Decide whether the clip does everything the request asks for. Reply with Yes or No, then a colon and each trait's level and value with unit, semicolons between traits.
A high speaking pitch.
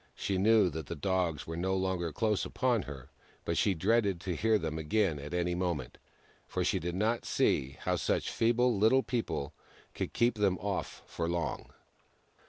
No: very low, 95 Hz